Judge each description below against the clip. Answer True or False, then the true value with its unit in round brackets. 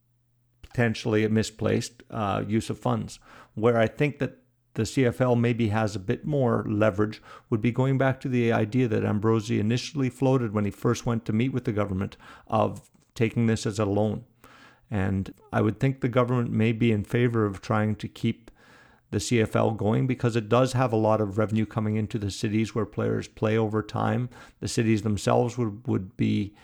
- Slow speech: False (190 wpm)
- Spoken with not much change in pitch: True (2.0 semitones)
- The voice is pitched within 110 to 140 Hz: True (115 Hz)